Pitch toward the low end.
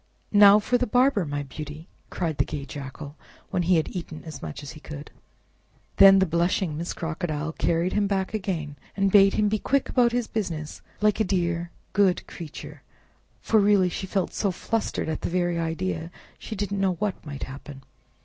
No: medium, 180 Hz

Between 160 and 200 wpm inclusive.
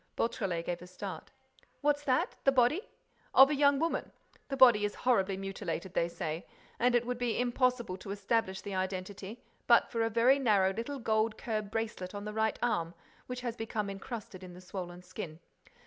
Yes: average, 180 wpm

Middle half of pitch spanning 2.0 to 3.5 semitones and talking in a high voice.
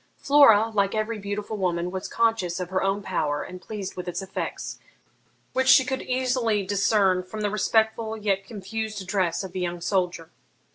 Yes: average, 3.1 semitones; high, 200 Hz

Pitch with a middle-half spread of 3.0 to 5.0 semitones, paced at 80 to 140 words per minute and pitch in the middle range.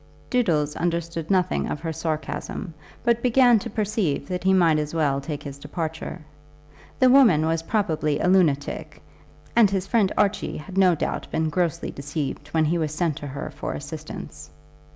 No: average, 4.2 semitones; average, 170 wpm; medium, 165 Hz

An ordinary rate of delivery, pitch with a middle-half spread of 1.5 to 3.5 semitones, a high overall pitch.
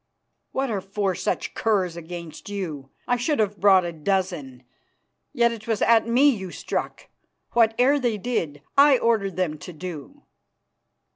No: average, 150 wpm; average, 5.1 semitones; high, 200 Hz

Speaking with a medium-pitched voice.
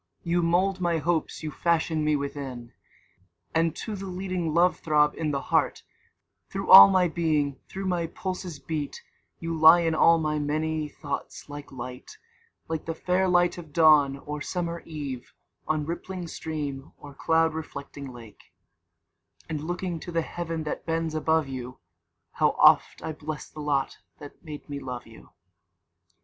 Yes: medium, 160 Hz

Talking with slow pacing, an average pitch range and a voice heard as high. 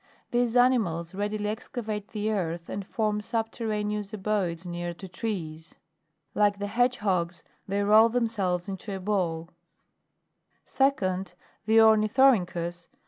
Yes: slow, 130 wpm; average, 3.6 semitones; high, 205 Hz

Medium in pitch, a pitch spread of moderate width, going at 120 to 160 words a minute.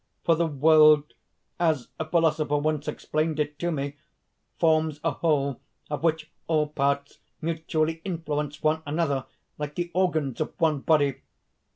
No: medium, 155 Hz; narrow, 1.8 semitones; average, 145 wpm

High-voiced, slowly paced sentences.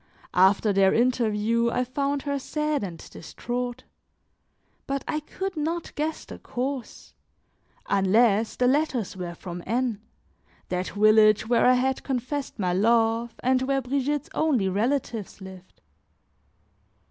Yes: high, 240 Hz; slow, 125 wpm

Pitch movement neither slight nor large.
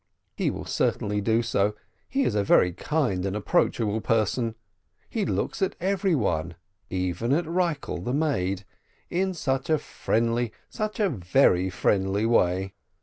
No: wide, 8.1 semitones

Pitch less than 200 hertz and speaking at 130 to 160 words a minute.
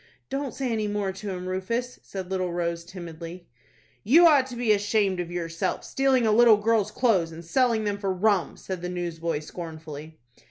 No: high, 190 Hz; average, 185 wpm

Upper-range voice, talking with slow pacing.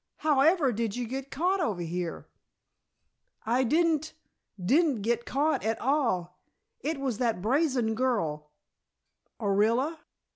Yes: very high, 250 Hz; slow, 120 wpm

